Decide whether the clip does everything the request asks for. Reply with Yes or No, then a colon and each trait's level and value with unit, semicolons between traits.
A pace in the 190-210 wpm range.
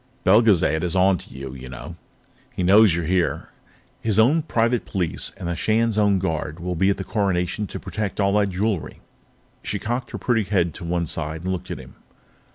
Yes: average, 200 wpm